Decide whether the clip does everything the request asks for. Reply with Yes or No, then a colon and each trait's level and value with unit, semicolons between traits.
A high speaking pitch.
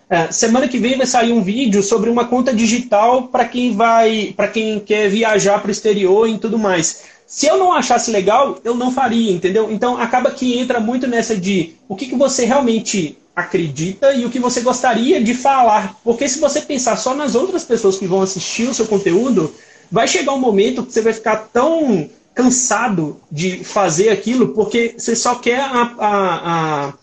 Yes: high, 230 Hz